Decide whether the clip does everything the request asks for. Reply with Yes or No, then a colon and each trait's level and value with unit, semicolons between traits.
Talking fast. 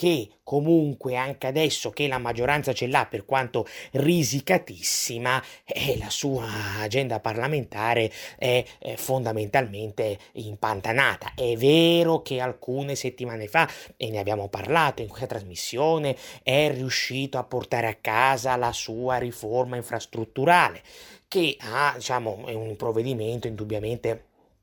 No: average, 120 wpm